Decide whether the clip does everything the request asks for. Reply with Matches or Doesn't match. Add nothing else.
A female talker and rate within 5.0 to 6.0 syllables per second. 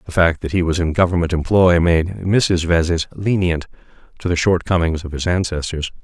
Doesn't match